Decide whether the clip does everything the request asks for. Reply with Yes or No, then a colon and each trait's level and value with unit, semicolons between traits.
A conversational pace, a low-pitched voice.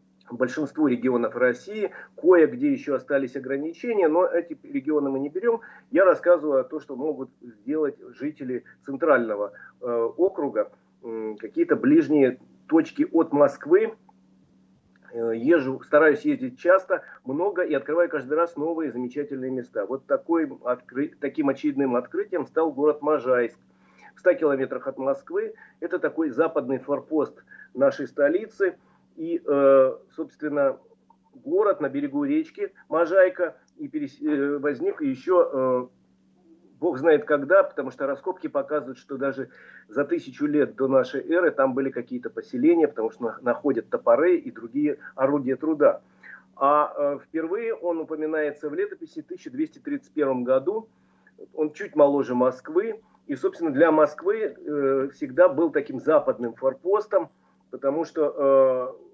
No: average, 135 wpm; medium, 155 Hz